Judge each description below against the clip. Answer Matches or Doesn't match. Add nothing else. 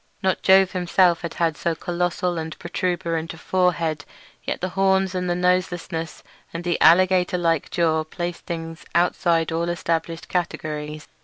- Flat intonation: Matches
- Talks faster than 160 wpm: Doesn't match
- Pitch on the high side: Doesn't match